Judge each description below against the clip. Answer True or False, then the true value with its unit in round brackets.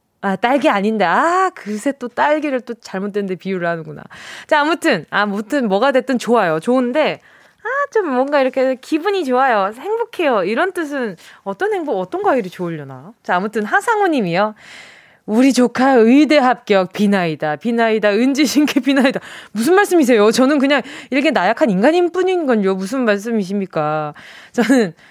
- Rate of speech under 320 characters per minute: False (350 characters per minute)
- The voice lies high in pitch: True (250 Hz)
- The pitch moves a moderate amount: False (6.4 semitones)